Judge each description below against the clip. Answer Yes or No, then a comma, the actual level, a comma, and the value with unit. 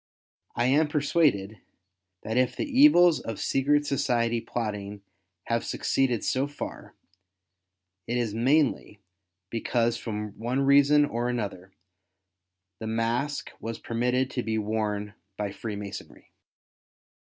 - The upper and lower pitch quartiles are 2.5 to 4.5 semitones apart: Yes, average, 4.1 semitones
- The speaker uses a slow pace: Yes, slow, 115 wpm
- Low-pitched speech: Yes, low, 120 Hz